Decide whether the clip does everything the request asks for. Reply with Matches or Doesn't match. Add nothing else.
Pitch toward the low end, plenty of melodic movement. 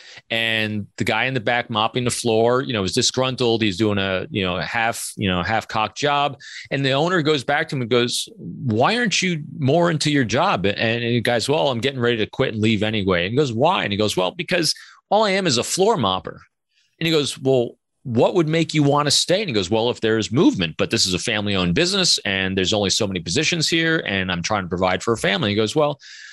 Matches